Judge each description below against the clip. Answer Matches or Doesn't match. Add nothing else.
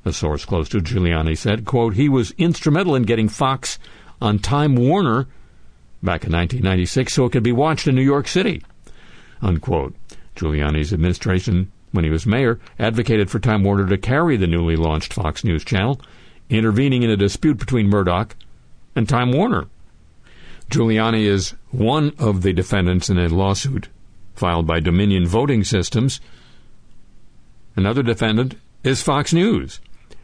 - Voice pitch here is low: Matches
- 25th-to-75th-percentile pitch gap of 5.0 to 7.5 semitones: Matches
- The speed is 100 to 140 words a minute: Doesn't match